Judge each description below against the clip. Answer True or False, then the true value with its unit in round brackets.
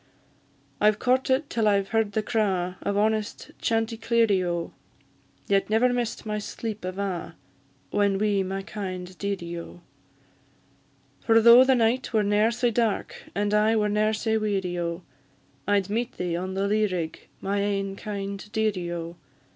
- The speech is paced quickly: False (155 wpm)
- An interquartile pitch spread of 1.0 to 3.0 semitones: True (2.5 semitones)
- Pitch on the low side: False (205 Hz)